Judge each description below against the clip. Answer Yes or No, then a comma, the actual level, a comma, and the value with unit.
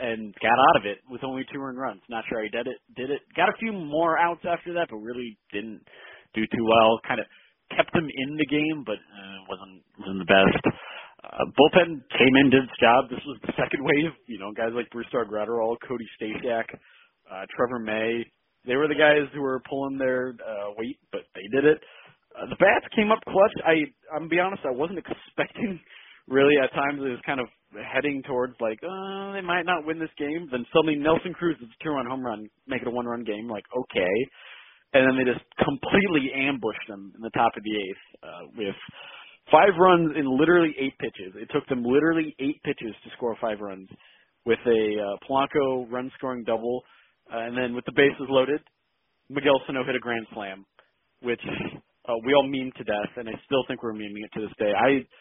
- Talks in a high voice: No, low, 130 Hz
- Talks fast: Yes, fast, 215 wpm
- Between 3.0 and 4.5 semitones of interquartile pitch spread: No, average, 4.9 semitones